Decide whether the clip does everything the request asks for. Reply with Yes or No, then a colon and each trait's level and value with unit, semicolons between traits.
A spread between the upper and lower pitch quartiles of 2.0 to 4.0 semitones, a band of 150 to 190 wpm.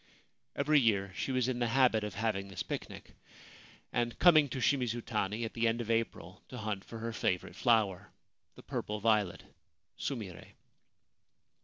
Yes: average, 2.7 semitones; average, 160 wpm